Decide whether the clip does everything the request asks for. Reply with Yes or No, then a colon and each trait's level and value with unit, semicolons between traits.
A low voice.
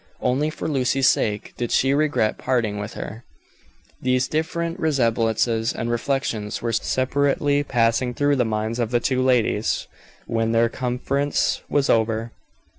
Yes: low, 125 Hz